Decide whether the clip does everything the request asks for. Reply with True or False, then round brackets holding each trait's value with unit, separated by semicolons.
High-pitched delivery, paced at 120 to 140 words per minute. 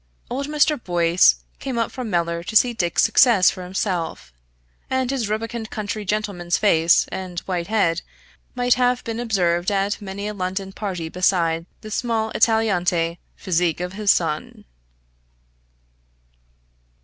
True (195 Hz; 135 wpm)